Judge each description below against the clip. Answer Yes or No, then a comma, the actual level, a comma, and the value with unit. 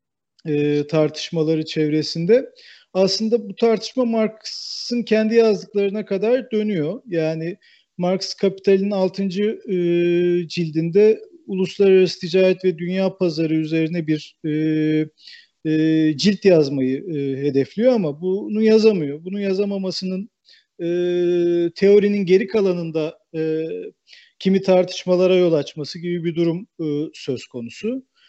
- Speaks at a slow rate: Yes, slow, 90 wpm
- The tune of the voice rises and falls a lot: No, average, 4.4 semitones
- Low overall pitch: No, medium, 185 Hz